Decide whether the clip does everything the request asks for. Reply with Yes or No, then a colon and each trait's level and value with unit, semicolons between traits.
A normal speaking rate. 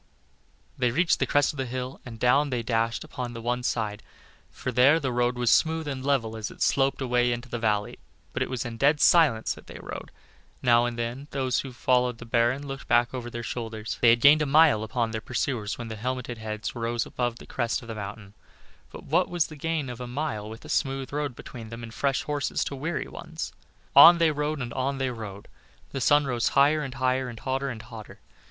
No: fast, 225 wpm